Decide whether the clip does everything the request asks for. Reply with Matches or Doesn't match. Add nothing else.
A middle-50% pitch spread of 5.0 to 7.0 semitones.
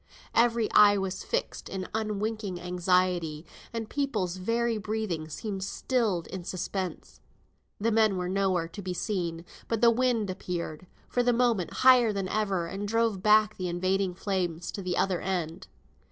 Doesn't match